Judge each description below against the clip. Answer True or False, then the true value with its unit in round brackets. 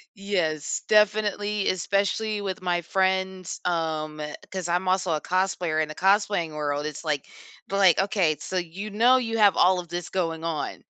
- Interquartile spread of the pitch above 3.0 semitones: True (3.5 semitones)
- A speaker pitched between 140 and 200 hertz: True (185 Hz)